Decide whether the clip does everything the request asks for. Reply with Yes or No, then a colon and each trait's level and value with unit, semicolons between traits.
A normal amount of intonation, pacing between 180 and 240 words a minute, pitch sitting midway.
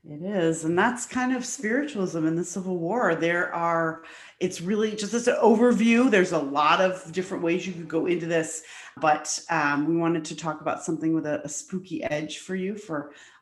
Yes: average, 3.1 semitones; fast, 205 wpm; medium, 170 Hz